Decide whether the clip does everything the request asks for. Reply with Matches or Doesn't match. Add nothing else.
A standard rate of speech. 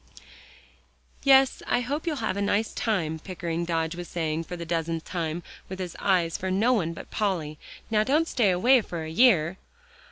Matches